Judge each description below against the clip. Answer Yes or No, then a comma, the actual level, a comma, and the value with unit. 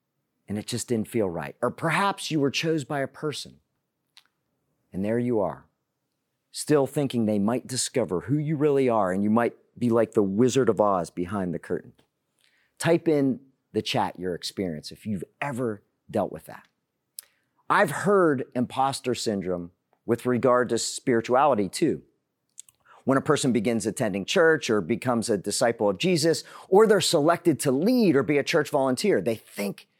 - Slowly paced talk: No, average, 170 wpm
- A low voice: Yes, low, 125 Hz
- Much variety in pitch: No, average, 4.9 semitones